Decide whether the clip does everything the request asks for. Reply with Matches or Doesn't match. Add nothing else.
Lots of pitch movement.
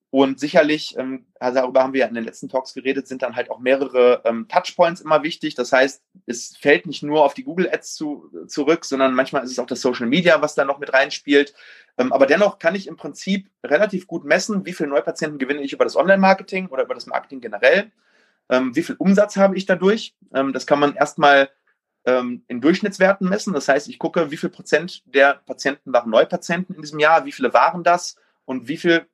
Matches